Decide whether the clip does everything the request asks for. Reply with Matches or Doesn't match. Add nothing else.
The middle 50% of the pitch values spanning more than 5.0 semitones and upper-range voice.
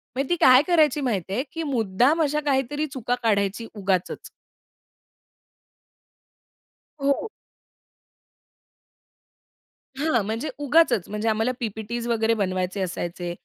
Matches